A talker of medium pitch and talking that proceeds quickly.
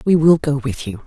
Yes: medium, 145 Hz; fast, 280 wpm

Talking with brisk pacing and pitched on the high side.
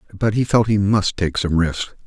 No: fast, 230 wpm; low, 100 Hz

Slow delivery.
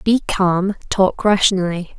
Yes: slow, 120 wpm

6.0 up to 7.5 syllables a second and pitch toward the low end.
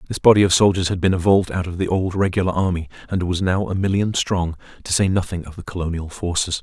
Yes: 6.3 syllables/s; very low, 90 Hz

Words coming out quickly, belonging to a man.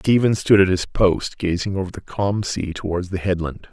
Yes: fast, 210 wpm; male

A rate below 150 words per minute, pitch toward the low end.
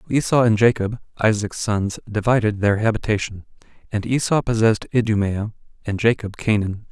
Yes: average, 140 wpm; low, 110 Hz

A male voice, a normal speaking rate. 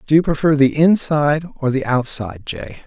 Yes: male; average, 190 wpm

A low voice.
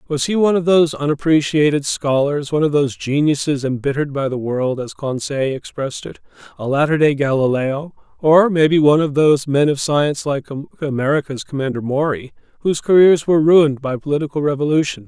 No: medium, 145 Hz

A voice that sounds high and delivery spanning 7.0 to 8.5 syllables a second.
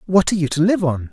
No: medium, 170 Hz; 7.2 syllables/s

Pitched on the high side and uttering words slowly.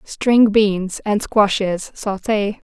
Yes: high, 205 Hz; slow, 110 wpm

